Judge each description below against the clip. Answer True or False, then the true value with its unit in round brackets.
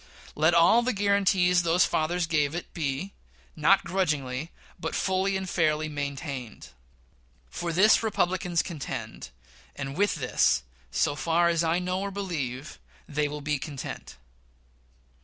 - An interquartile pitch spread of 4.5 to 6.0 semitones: False (4.1 semitones)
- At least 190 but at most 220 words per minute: False (135 wpm)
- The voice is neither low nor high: True (165 Hz)